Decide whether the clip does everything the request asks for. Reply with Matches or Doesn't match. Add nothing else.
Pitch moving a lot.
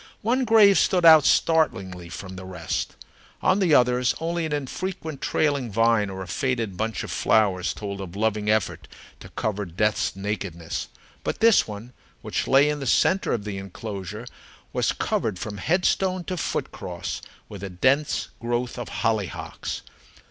Matches